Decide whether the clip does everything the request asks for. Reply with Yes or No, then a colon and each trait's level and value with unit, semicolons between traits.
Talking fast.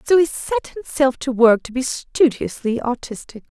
No: average, 165 wpm